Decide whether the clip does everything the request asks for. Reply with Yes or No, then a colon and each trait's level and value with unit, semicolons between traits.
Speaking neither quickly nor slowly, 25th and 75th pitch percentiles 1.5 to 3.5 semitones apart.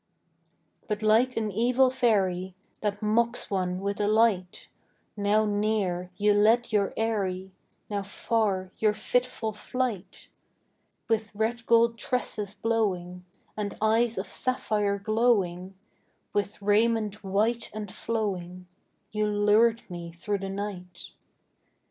No: slow, 120 wpm; narrow, 2.6 semitones